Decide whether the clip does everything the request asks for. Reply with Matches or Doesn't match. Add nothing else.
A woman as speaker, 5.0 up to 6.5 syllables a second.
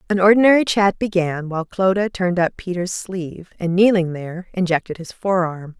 Matches